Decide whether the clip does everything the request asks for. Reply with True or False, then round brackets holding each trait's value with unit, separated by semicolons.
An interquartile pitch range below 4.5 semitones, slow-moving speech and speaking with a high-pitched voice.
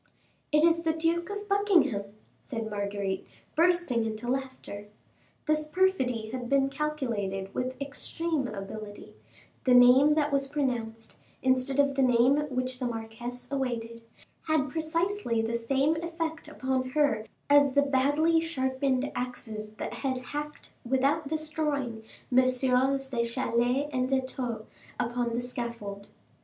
True (4.1 semitones; 130 wpm; 260 Hz)